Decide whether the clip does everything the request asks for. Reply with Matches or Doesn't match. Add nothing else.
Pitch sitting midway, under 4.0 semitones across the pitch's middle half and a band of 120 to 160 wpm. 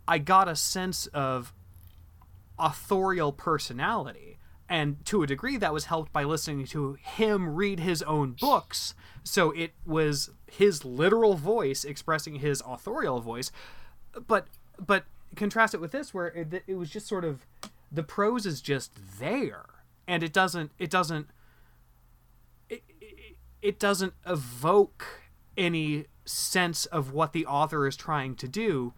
Doesn't match